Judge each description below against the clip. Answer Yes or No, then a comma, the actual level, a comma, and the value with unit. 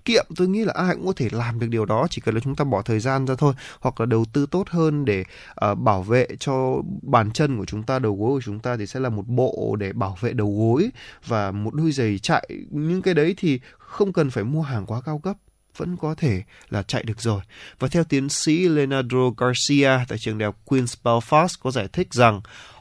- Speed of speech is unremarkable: Yes, average, 240 wpm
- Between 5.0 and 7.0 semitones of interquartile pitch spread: Yes, average, 5.3 semitones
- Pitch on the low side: Yes, low, 130 Hz